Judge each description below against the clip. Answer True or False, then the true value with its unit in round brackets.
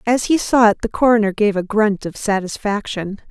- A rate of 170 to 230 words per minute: True (200 wpm)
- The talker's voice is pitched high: True (210 Hz)